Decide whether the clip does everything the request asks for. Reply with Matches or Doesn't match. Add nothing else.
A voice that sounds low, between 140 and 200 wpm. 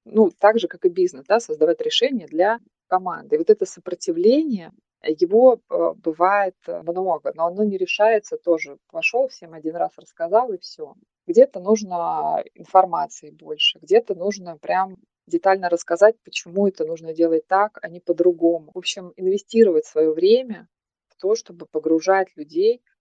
Doesn't match